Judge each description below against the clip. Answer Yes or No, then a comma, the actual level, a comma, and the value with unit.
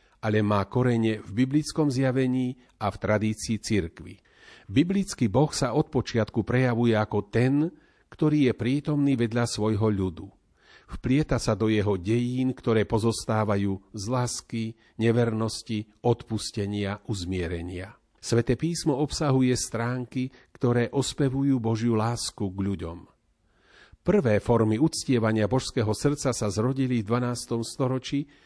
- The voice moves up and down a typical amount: Yes, average, 3.3 semitones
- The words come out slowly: No, average, 120 wpm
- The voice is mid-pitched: No, low, 115 Hz